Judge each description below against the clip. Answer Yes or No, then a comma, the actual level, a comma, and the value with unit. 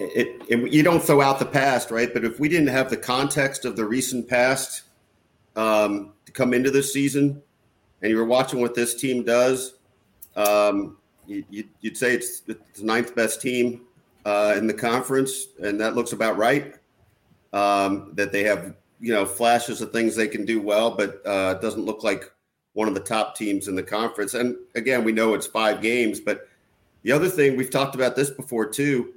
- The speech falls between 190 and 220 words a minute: Yes, average, 200 wpm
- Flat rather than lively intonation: No, average, 3.6 semitones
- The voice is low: Yes, low, 120 Hz